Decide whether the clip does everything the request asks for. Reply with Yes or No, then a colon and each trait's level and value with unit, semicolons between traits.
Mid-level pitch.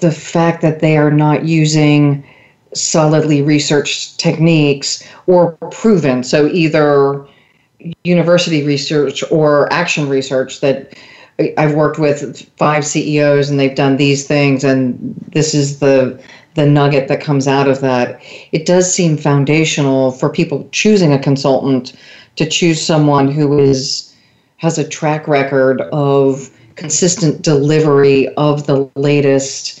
Yes: medium, 145 Hz